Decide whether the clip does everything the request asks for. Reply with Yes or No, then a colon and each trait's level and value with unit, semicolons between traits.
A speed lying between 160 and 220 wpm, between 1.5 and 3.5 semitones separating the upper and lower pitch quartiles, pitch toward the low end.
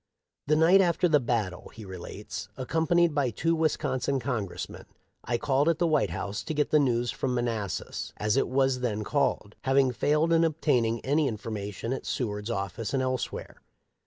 No: average, 180 wpm; average, 5.1 semitones; low, 130 Hz